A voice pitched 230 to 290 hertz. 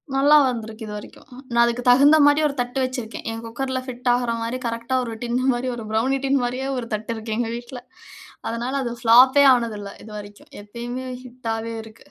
Yes: high, 240 Hz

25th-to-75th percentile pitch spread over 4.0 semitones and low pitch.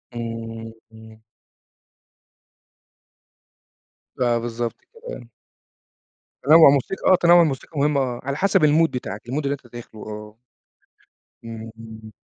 Yes: average, 4.7 semitones; low, 120 Hz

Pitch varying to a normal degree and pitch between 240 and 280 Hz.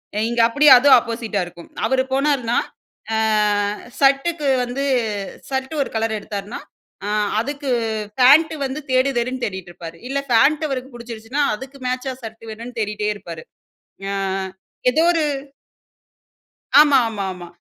Yes: average, 4.0 semitones; high, 245 Hz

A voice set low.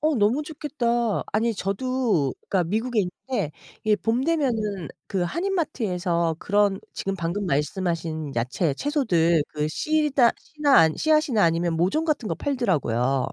No: high, 205 Hz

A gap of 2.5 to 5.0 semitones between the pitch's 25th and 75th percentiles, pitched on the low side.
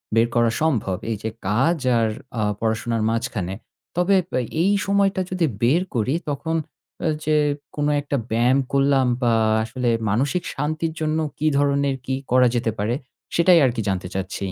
No: wide, 5.6 semitones; low, 130 Hz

